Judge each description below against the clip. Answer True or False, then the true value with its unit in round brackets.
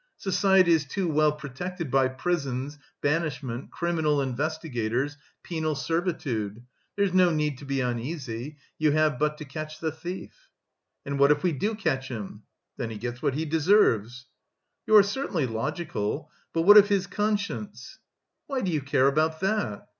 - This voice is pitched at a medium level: True (150 Hz)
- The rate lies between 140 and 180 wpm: True (160 wpm)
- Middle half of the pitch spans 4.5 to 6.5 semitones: True (4.8 semitones)